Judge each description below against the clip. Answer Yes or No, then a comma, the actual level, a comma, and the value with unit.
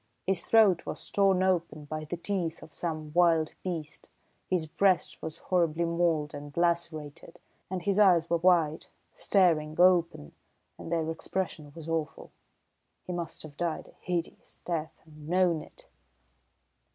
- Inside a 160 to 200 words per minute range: No, average, 145 wpm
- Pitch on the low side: No, medium, 170 Hz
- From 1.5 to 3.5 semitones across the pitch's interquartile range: Yes, narrow, 2.5 semitones